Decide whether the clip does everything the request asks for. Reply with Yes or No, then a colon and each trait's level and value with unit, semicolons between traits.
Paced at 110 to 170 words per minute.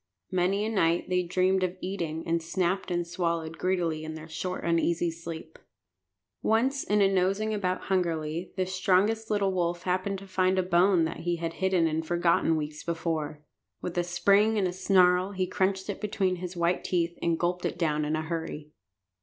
No: average, 185 wpm